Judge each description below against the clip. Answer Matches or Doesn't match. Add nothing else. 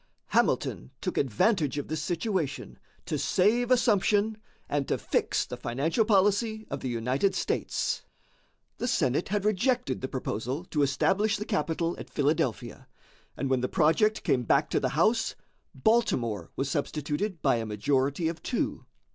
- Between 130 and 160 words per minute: Matches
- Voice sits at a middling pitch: Matches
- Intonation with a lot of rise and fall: Matches